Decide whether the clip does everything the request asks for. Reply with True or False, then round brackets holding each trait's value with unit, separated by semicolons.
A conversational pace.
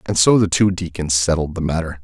False (235 wpm)